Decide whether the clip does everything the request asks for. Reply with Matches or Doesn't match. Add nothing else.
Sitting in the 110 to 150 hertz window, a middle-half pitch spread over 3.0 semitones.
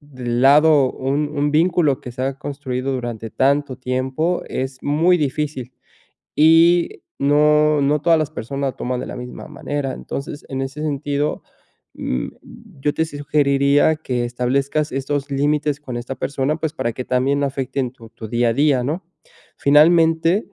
Doesn't match